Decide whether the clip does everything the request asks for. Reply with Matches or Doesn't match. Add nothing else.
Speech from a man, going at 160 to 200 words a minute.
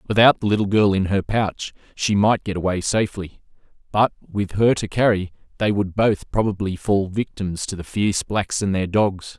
Matches